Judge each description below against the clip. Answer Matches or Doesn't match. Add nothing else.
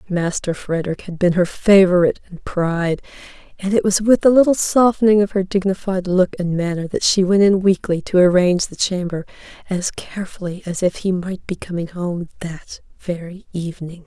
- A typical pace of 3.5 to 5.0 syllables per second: Doesn't match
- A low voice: Doesn't match